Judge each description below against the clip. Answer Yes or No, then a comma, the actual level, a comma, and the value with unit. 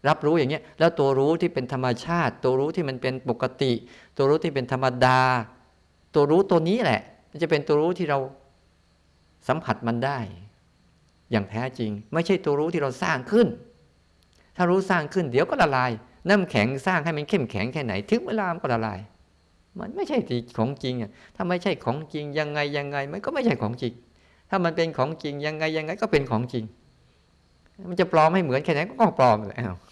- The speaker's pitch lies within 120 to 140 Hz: Yes, low, 135 Hz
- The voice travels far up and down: Yes, wide, 6.4 semitones